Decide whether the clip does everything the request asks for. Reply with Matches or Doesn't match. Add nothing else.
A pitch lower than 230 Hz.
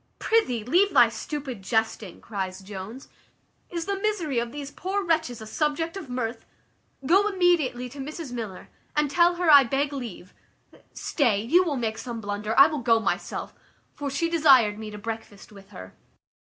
Doesn't match